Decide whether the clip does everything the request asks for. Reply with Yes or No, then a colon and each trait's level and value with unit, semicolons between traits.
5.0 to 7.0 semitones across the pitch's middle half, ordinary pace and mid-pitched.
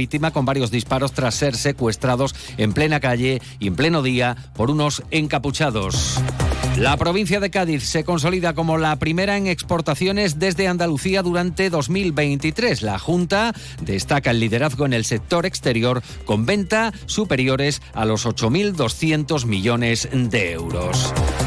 Yes: average, 5.3 semitones; average, 135 wpm; medium, 145 Hz